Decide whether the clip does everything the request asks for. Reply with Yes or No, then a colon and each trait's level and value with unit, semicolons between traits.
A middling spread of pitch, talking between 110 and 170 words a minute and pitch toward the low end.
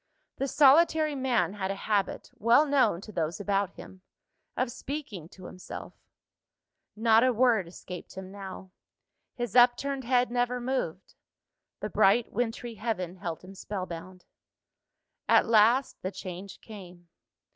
No: average, 4.8 semitones; slow, 135 wpm; high, 215 Hz